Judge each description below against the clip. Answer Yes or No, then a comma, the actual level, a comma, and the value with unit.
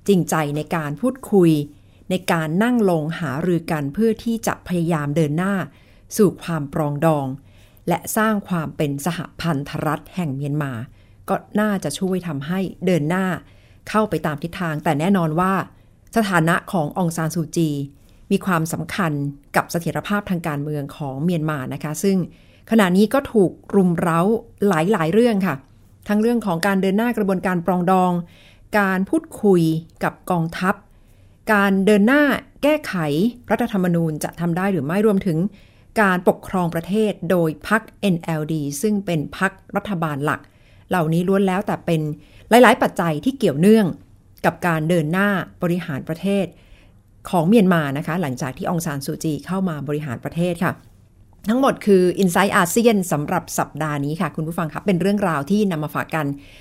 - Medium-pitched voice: Yes, medium, 175 Hz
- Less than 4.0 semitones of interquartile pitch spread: No, average, 4.7 semitones